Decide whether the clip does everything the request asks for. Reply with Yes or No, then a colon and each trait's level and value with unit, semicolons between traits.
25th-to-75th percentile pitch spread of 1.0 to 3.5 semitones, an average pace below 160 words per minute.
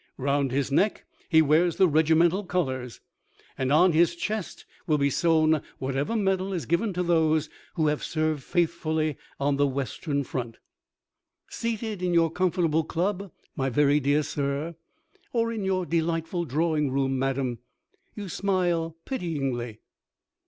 No: average, 4.0 semitones; average, 140 wpm